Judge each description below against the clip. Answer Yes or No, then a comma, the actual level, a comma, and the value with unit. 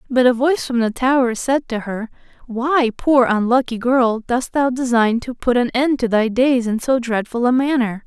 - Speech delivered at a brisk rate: Yes, fast, 210 wpm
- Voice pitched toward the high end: Yes, high, 245 Hz